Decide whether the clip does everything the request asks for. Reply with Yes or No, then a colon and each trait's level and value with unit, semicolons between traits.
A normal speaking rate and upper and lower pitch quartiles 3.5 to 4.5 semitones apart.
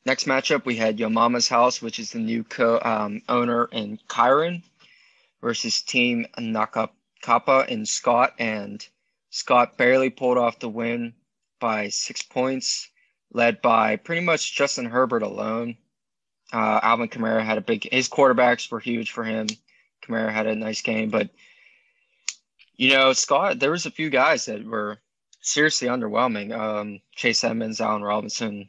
No: average, 155 wpm; narrow, 2.6 semitones